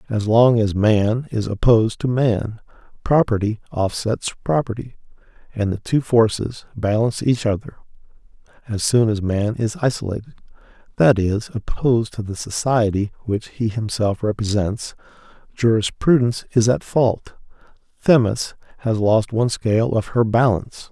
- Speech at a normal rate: No, slow, 130 wpm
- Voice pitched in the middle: No, low, 115 Hz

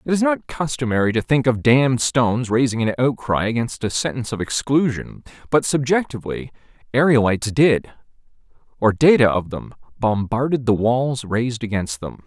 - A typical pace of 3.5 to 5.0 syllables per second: No, 5.3 syllables/s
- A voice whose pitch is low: Yes, low, 120 Hz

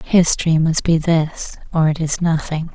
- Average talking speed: Yes, average, 175 wpm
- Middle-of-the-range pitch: Yes, medium, 160 Hz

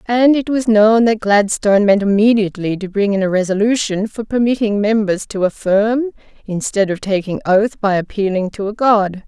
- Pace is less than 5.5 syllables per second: Yes, 5.1 syllables/s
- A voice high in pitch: Yes, high, 210 Hz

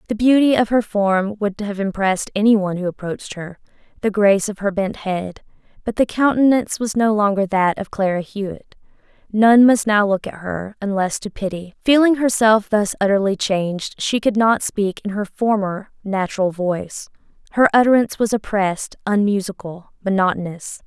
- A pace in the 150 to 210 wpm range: Yes, average, 165 wpm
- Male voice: No, female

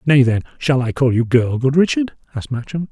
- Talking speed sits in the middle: No, fast, 225 wpm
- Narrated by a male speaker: Yes, male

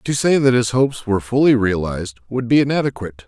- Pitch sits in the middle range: No, low, 120 Hz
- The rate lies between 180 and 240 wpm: Yes, average, 200 wpm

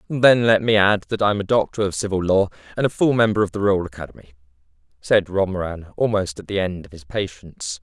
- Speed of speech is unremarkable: No, fast, 215 wpm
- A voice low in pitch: Yes, low, 100 Hz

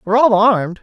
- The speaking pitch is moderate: No, high, 215 Hz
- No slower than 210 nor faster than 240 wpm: Yes, fast, 215 wpm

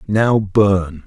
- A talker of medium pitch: No, low, 100 Hz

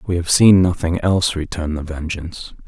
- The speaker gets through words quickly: No, average, 180 wpm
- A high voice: No, very low, 85 Hz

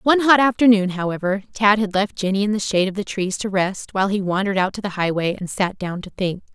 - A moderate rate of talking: No, fast, 255 wpm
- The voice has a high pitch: Yes, high, 200 Hz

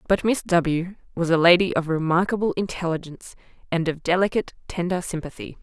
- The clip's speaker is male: No, female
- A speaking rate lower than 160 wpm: Yes, average, 150 wpm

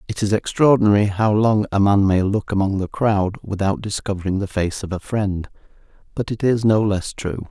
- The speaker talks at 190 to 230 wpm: Yes, average, 200 wpm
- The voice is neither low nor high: No, low, 105 Hz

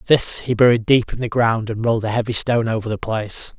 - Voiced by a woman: No, male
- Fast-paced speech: Yes, fast, 250 wpm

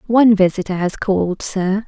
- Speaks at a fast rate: No, average, 160 wpm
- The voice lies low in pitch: No, high, 200 Hz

